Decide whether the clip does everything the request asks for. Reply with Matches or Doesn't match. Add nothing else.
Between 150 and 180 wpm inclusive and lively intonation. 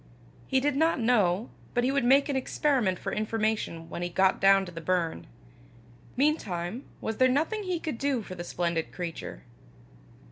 Matches